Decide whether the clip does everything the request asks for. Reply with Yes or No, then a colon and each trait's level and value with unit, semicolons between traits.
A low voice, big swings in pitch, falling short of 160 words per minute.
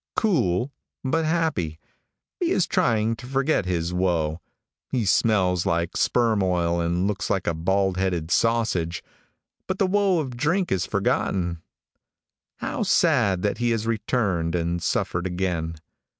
Yes: very low, 95 Hz; wide, 6.1 semitones; average, 140 wpm